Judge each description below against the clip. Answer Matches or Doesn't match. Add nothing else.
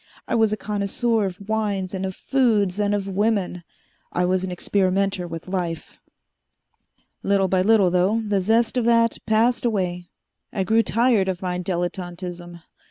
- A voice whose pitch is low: Doesn't match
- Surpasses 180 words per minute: Doesn't match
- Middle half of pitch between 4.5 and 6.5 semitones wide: Doesn't match